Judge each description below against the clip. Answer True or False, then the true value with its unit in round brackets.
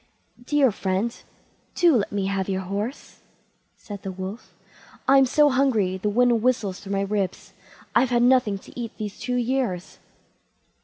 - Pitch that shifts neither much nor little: True (4.3 semitones)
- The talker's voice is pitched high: True (215 Hz)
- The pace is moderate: True (155 wpm)